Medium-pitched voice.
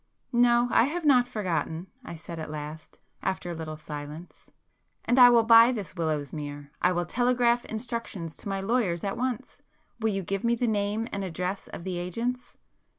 No: high, 195 Hz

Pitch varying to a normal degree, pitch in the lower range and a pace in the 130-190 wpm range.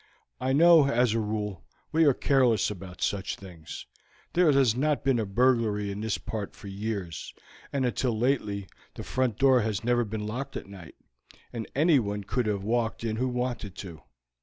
Yes: average, 4.1 semitones; low, 115 Hz; average, 180 wpm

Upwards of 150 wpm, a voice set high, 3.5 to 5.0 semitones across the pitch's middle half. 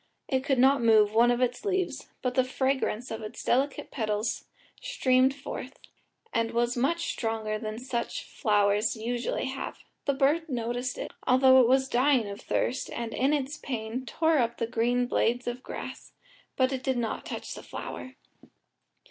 No: average, 165 wpm; very high, 250 Hz; narrow, 2.6 semitones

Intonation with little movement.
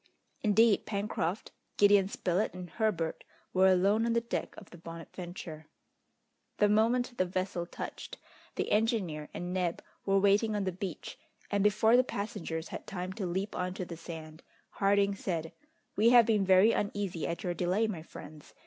No: average, 3.1 semitones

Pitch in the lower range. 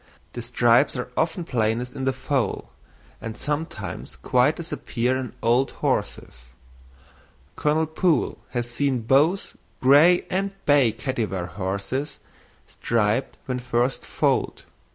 Yes: low, 130 Hz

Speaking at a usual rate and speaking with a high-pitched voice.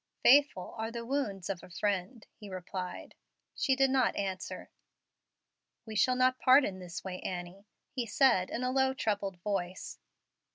Yes: average, 160 wpm; high, 205 Hz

